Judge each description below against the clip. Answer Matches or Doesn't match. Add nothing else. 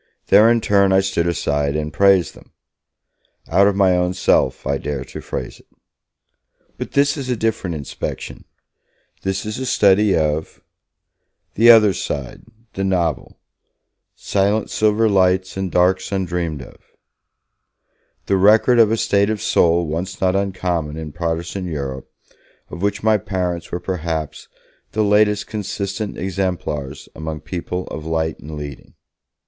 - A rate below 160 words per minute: Matches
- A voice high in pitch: Doesn't match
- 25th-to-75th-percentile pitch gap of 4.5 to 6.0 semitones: Doesn't match